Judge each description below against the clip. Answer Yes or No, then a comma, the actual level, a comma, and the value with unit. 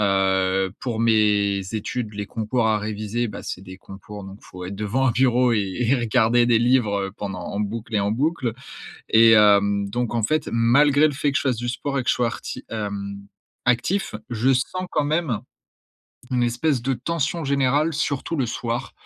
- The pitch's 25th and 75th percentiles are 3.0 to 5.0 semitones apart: Yes, average, 4.1 semitones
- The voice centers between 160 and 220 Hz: No, low, 115 Hz